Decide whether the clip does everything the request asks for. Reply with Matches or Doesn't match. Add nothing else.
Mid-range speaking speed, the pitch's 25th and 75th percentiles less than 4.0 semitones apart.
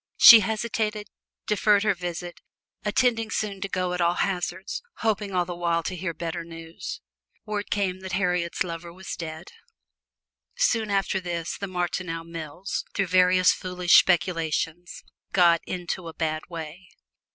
Matches